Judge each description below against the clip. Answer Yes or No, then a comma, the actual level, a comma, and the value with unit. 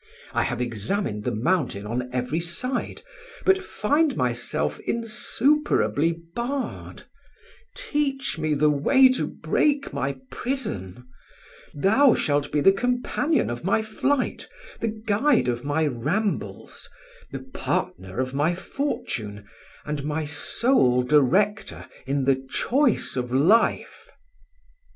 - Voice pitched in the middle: Yes, medium, 165 Hz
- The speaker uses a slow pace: Yes, slow, 115 wpm